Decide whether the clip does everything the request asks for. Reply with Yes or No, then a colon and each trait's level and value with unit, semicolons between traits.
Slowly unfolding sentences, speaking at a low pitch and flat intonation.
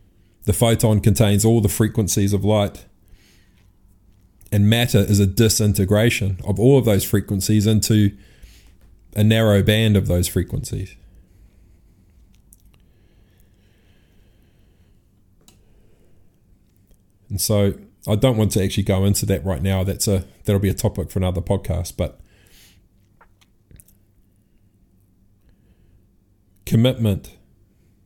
Yes: slow, 105 wpm; low, 100 Hz; narrow, 1.9 semitones